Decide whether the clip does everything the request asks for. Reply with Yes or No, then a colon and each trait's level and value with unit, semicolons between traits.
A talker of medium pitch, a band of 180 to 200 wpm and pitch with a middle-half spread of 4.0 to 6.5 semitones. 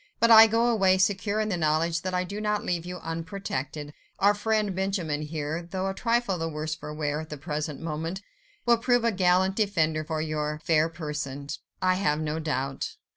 Yes: medium, 170 Hz; average, 195 wpm; average, 4.6 semitones